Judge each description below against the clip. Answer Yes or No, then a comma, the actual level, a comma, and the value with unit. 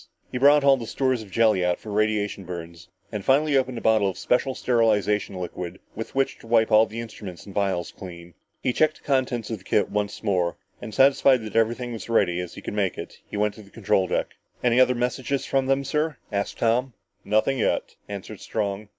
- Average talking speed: No, fast, 225 wpm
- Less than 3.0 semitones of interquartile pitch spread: No, average, 4.1 semitones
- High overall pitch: No, low, 110 Hz